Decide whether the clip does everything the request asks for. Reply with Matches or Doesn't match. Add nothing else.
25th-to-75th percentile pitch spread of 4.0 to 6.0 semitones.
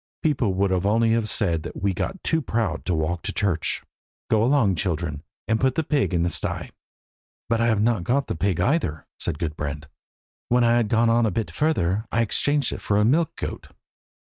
Matches